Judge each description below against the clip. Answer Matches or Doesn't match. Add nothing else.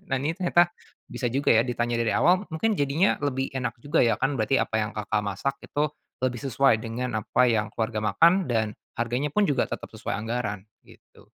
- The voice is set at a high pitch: Doesn't match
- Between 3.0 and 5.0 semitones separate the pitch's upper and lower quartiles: Matches